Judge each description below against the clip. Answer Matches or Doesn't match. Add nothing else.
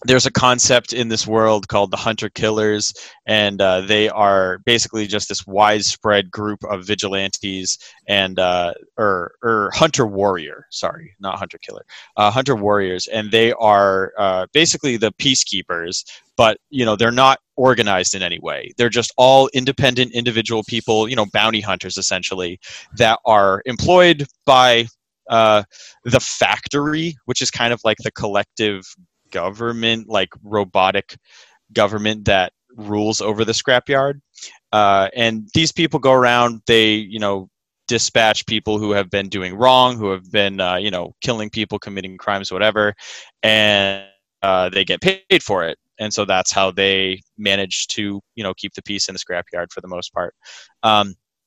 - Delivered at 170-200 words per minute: Doesn't match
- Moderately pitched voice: Doesn't match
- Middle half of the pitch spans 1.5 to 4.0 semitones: Matches